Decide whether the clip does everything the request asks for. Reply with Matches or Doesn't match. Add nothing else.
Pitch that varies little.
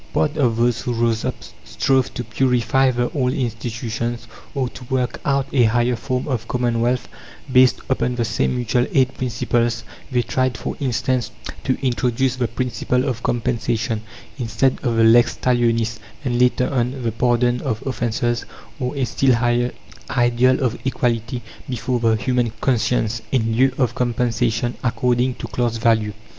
Matches